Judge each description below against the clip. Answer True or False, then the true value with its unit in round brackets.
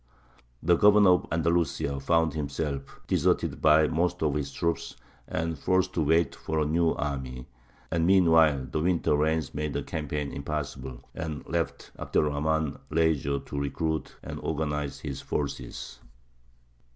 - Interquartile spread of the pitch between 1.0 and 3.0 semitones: True (2.5 semitones)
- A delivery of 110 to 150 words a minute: True (145 wpm)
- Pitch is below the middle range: True (75 Hz)